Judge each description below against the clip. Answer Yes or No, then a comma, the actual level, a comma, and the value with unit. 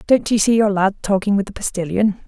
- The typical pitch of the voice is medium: No, high, 205 Hz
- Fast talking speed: Yes, fast, 235 wpm